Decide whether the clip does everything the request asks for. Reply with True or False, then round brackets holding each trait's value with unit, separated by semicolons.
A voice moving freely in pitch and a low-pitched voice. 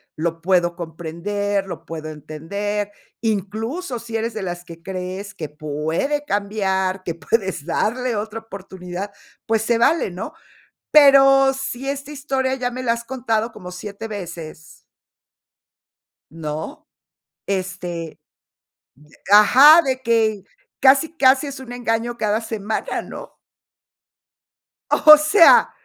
False (5.8 semitones; 210 Hz)